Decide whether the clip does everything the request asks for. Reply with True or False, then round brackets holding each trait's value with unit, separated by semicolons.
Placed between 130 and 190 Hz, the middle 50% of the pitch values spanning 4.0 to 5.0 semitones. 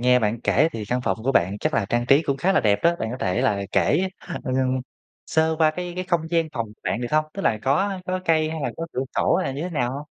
False (140 Hz; 5.4 semitones)